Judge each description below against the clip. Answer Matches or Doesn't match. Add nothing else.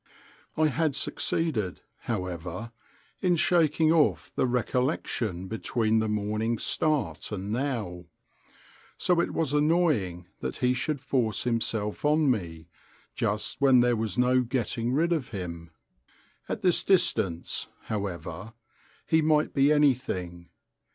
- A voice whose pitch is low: Matches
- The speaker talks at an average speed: Doesn't match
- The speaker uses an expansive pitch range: Matches